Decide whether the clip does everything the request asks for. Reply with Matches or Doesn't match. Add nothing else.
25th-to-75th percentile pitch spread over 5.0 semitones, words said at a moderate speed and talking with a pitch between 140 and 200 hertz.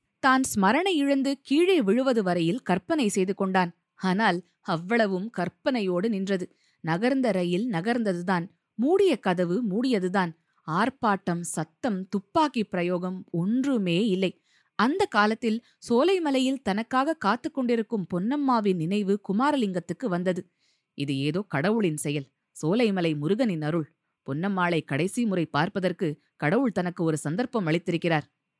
Matches